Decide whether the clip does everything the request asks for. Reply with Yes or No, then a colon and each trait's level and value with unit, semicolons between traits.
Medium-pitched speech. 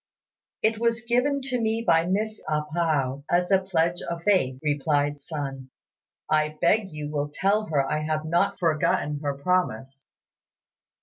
Yes: medium, 160 Hz